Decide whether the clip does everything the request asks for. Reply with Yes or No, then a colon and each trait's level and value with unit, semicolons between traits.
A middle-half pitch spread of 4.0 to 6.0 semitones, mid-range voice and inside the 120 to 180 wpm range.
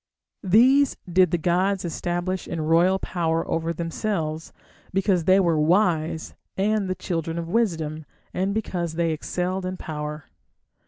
No: narrow, 2.6 semitones; medium, 175 Hz; average, 140 wpm